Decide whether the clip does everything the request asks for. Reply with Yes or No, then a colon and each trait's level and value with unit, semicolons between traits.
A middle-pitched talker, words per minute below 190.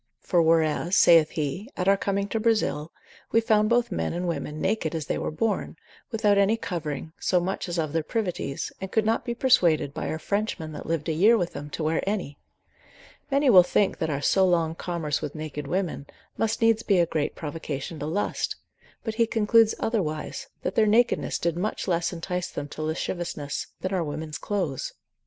No: medium, 175 Hz; average, 195 wpm